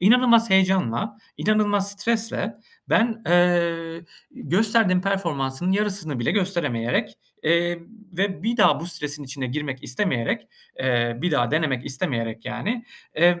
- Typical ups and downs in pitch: No, wide, 6.8 semitones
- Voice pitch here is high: No, medium, 175 Hz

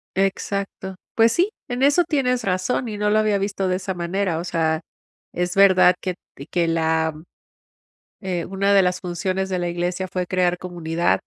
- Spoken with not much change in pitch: Yes, narrow, 2.2 semitones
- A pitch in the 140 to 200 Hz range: Yes, medium, 185 Hz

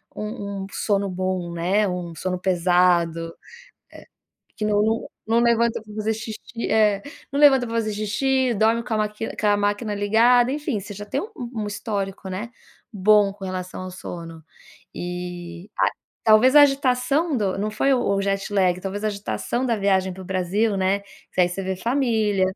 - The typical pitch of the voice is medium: No, high, 205 Hz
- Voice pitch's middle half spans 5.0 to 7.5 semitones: No, average, 3.3 semitones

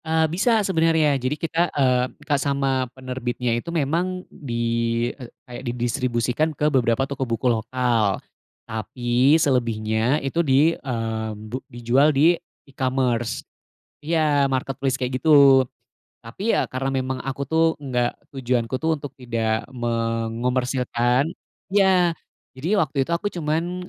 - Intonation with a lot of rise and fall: No, average, 4.2 semitones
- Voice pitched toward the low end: Yes, low, 130 Hz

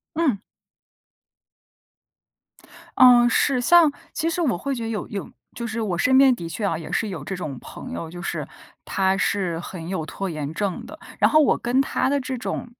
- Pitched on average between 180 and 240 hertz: Yes, high, 215 Hz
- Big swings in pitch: Yes, wide, 6.6 semitones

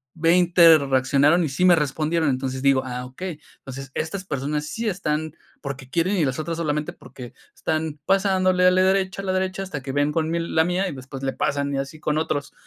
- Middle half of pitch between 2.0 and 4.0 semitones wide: No, average, 4.6 semitones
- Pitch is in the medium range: Yes, medium, 155 Hz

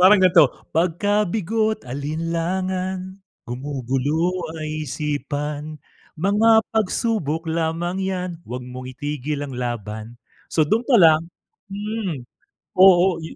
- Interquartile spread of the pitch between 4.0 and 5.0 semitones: Yes, average, 4.6 semitones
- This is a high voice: No, medium, 165 Hz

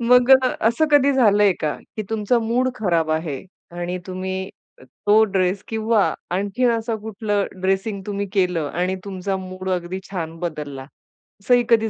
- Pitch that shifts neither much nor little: Yes, average, 3.6 semitones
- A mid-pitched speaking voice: No, high, 195 Hz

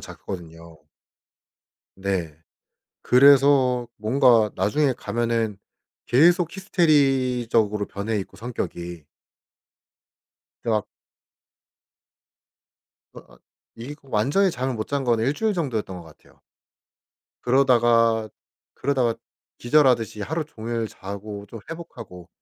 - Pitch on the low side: Yes, low, 115 Hz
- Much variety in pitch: No, average, 4.8 semitones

